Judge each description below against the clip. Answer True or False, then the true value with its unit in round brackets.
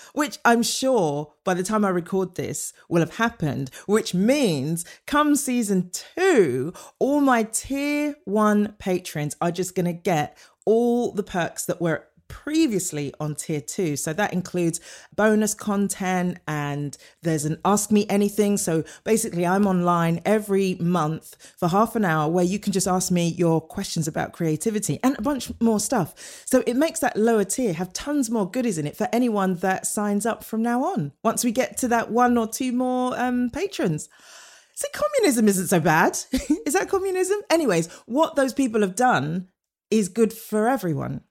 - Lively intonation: True (5.8 semitones)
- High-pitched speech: True (205 Hz)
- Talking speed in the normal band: True (175 wpm)